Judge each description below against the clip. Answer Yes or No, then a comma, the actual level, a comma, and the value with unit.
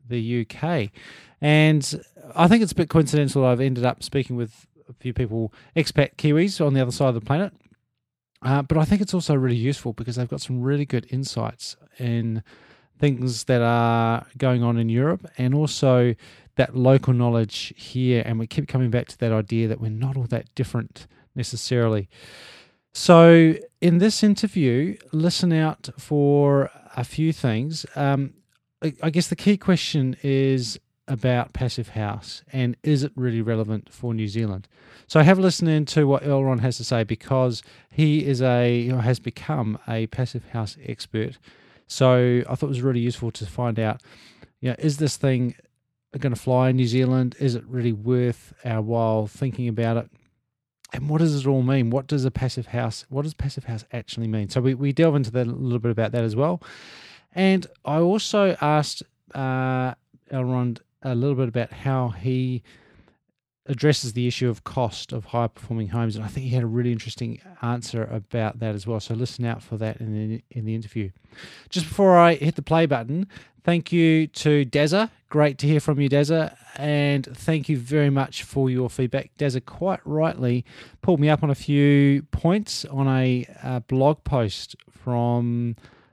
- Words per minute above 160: Yes, average, 185 wpm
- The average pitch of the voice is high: No, low, 130 Hz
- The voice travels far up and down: No, average, 3.8 semitones